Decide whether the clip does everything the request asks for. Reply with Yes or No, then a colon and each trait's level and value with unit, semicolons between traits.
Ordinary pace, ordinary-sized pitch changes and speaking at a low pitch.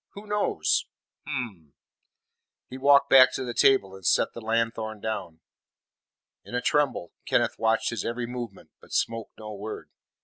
Yes: average, 150 wpm; average, 3.4 semitones; low, 115 Hz